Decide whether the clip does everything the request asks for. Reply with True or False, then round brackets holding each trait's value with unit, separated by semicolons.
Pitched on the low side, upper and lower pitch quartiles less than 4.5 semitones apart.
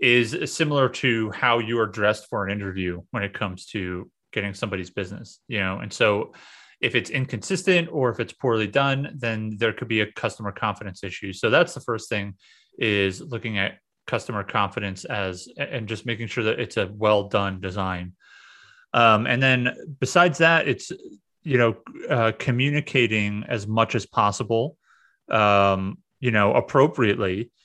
True (110 Hz; 3.7 semitones)